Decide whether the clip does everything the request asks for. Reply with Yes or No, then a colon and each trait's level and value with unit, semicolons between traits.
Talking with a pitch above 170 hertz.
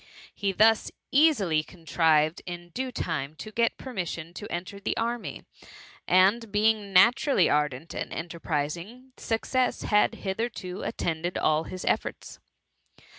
Yes: medium, 185 Hz